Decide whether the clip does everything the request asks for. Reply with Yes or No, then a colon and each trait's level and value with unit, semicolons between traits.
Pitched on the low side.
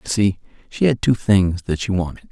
Yes: low, 100 Hz